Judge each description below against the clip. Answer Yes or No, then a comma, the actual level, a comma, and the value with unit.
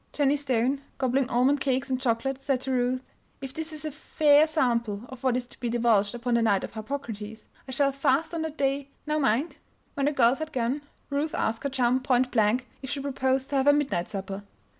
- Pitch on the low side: No, very high, 265 Hz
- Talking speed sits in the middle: No, fast, 220 wpm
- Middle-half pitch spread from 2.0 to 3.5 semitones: Yes, average, 2.9 semitones